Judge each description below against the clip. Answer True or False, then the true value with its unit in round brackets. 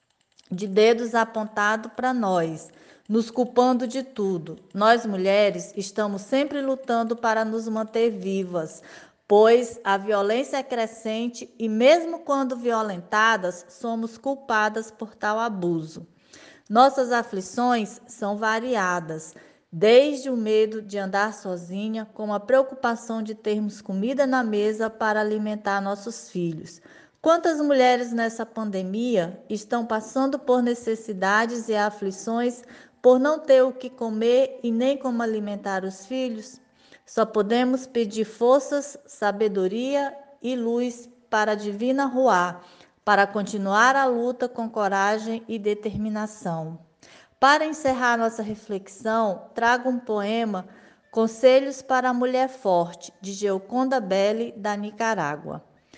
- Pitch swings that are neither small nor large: True (3.4 semitones)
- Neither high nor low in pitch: False (225 Hz)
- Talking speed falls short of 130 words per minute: True (120 wpm)